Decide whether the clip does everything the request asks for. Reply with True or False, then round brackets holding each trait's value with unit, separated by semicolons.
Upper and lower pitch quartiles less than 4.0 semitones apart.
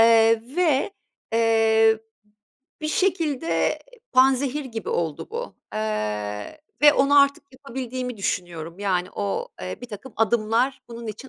False (4.5 semitones)